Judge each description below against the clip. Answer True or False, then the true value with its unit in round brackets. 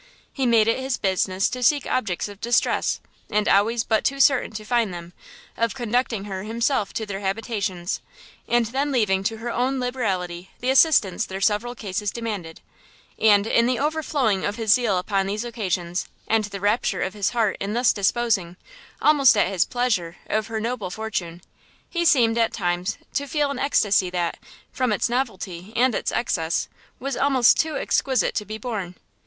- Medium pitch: False (220 Hz)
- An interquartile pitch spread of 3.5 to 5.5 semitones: True (4.2 semitones)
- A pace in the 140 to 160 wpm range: False (180 wpm)